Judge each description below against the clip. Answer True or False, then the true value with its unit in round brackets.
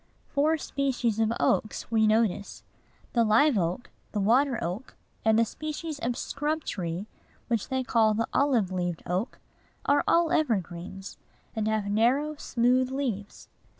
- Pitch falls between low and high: False (230 Hz)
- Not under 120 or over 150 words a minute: True (145 wpm)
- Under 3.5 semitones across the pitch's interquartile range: False (5.0 semitones)